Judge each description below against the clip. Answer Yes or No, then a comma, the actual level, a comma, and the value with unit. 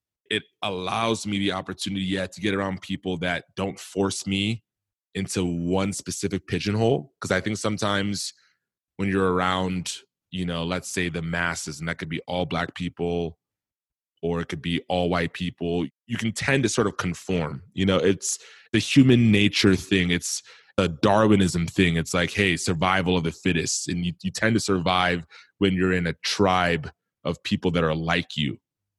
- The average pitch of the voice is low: Yes, very low, 95 Hz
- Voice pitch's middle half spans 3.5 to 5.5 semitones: No, narrow, 2.6 semitones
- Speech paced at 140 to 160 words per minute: No, average, 180 wpm